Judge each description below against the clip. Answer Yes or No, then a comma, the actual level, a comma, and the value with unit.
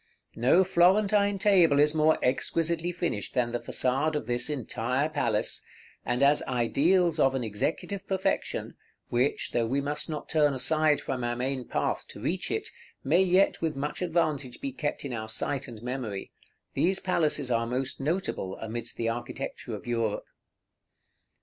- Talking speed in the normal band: Yes, average, 160 wpm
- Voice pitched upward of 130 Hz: Yes, medium, 140 Hz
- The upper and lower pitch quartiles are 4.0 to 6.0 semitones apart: Yes, wide, 5.5 semitones